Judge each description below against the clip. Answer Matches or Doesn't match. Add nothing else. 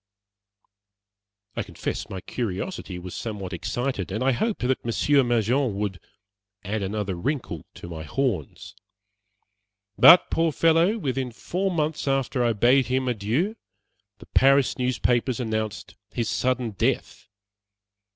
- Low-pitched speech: Matches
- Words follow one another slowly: Matches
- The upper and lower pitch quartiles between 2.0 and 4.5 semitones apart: Doesn't match